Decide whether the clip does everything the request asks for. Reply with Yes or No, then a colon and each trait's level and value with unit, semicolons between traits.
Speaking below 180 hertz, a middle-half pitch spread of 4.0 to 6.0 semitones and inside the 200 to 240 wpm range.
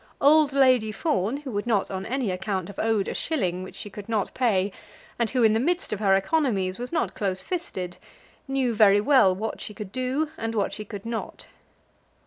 No: high, 220 Hz; average, 4.9 semitones; fast, 205 wpm